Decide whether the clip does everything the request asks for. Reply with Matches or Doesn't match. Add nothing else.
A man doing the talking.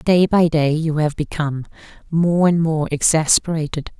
Doesn't match